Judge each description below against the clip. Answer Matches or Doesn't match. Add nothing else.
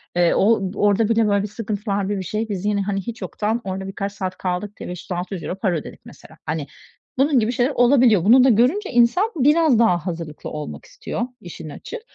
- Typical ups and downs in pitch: Matches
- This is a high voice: Matches